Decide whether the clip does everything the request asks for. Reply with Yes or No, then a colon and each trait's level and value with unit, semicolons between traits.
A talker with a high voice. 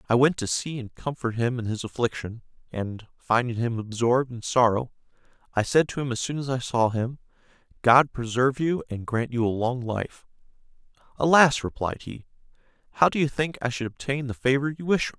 No: low, 125 Hz